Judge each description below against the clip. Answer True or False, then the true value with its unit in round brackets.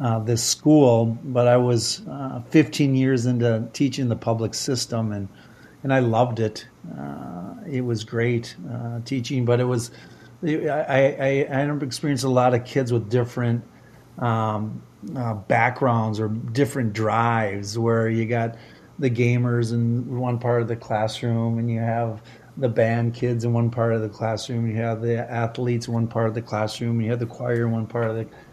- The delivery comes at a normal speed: True (185 wpm)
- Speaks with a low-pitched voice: True (120 Hz)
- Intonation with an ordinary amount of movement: False (1.5 semitones)